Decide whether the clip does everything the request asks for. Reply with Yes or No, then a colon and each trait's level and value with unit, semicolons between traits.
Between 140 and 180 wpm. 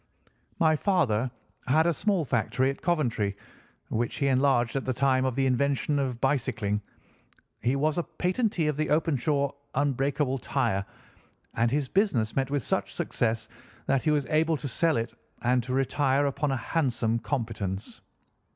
Yes: average, 160 wpm